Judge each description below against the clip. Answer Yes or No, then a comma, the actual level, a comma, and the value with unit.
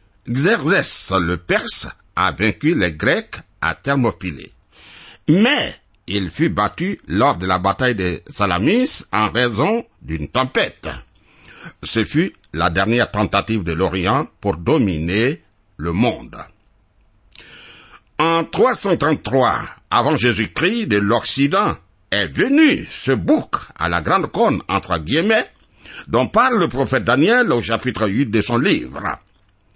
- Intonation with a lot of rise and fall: No, average, 5.0 semitones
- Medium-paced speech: No, slow, 125 wpm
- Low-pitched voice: Yes, low, 105 Hz